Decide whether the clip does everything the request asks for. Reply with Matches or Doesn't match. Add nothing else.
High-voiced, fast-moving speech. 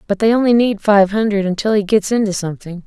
Matches